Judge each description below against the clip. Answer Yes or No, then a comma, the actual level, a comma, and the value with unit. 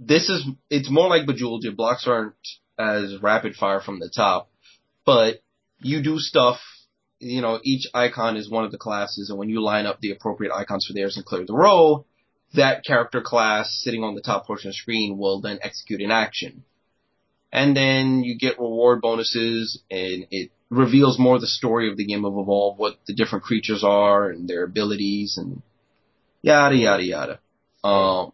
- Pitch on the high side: No, low, 110 Hz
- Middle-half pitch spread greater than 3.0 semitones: Yes, average, 3.5 semitones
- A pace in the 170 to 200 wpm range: Yes, average, 185 wpm